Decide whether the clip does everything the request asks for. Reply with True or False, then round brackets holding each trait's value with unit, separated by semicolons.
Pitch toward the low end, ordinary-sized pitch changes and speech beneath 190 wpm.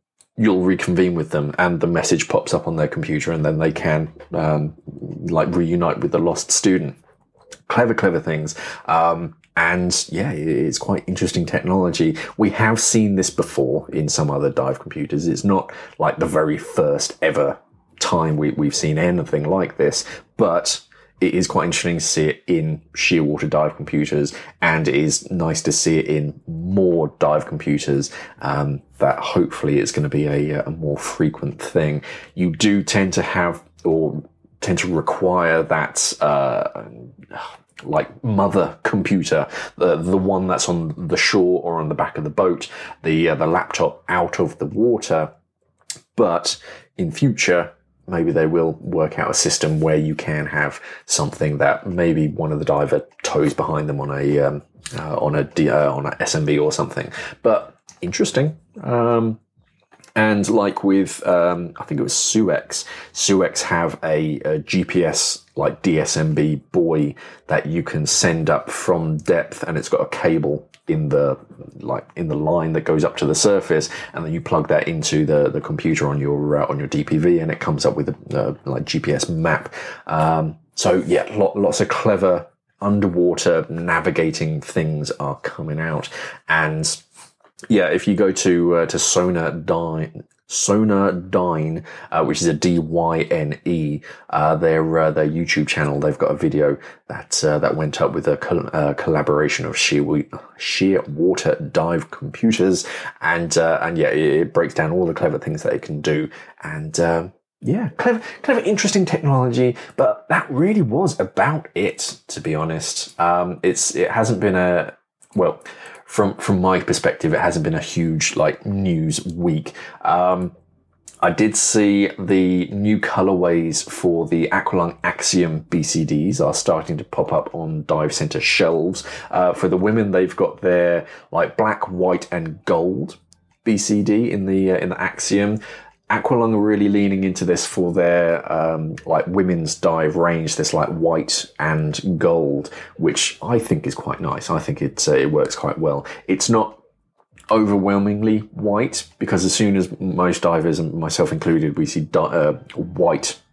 True (85 Hz; 4.2 semitones; 170 wpm)